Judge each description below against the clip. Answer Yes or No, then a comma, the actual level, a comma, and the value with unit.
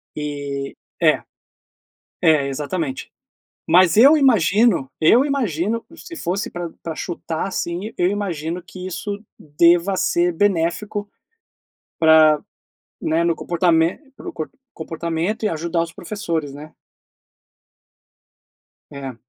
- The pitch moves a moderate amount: Yes, average, 4.0 semitones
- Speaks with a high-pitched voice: No, medium, 170 Hz